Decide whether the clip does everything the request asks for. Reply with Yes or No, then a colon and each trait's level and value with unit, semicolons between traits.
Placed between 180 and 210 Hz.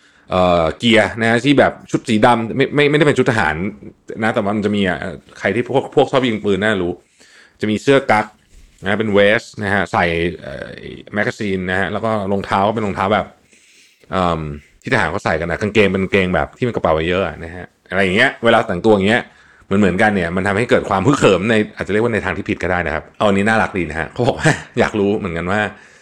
No: low, 100 Hz